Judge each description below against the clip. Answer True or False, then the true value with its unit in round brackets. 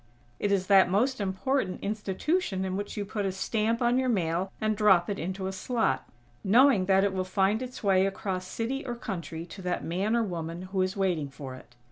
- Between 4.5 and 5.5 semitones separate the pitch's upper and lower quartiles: False (2.9 semitones)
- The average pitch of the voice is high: True (195 Hz)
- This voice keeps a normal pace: False (210 wpm)